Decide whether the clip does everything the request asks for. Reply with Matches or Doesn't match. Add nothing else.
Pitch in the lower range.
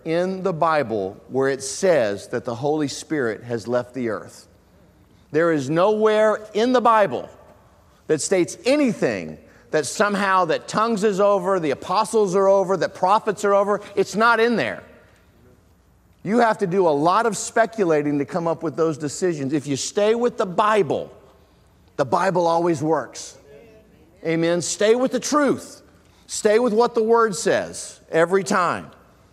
Doesn't match